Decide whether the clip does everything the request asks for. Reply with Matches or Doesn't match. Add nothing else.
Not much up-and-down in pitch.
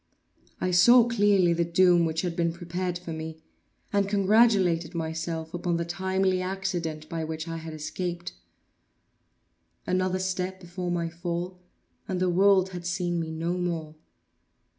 Matches